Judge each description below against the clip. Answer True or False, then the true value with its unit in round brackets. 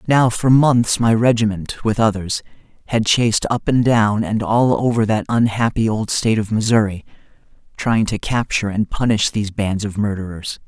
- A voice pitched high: False (110 Hz)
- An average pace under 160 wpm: False (170 wpm)